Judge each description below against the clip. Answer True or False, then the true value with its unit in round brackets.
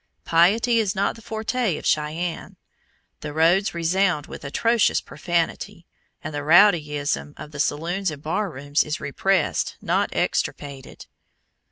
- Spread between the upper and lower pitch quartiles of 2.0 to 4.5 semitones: False (4.9 semitones)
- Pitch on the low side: False (170 Hz)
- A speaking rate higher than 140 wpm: False (135 wpm)